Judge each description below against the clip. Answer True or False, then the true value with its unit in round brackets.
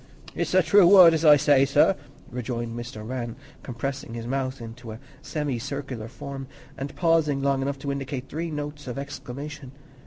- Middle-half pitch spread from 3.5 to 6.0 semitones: False (3.0 semitones)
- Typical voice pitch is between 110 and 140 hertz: True (135 Hz)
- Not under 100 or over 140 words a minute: False (165 wpm)